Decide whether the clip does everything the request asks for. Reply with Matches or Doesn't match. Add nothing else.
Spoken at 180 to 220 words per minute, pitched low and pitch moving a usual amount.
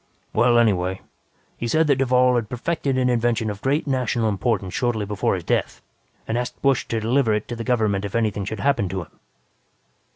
Matches